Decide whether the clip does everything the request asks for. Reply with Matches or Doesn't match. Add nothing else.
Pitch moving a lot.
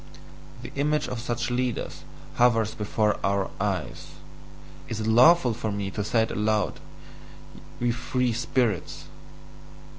Doesn't match